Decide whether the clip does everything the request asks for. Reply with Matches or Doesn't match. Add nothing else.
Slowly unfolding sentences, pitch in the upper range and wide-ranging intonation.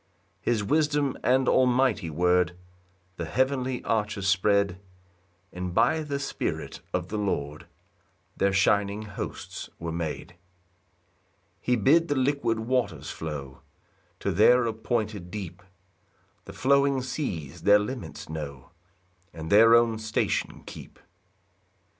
Doesn't match